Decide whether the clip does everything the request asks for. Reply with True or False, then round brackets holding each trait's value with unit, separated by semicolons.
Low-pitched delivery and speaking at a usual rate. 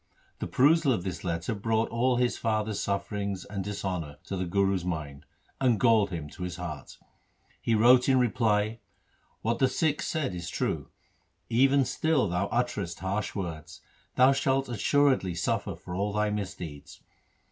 True (105 Hz; 160 wpm)